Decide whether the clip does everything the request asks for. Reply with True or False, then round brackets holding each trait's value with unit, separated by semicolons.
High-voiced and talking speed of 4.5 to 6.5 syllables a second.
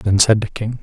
False (105 Hz; 5.1 syllables/s)